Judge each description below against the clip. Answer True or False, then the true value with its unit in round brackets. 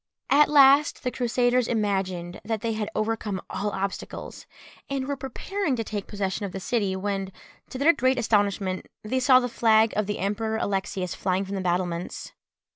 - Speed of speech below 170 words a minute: False (175 wpm)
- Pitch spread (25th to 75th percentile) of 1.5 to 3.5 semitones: False (4.3 semitones)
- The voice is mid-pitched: False (215 Hz)